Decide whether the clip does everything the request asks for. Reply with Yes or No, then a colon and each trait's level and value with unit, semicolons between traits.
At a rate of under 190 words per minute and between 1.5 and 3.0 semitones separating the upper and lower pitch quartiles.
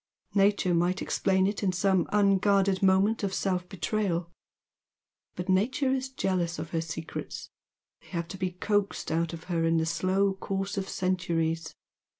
Yes: average, 155 wpm; average, 2.7 semitones